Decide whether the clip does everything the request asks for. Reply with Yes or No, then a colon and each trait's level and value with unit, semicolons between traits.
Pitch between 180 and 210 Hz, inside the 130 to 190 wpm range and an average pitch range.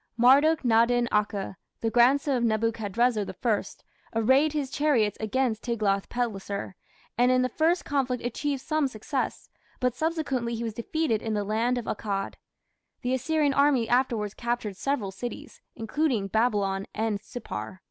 No: high, 240 Hz; average, 145 wpm; average, 3.7 semitones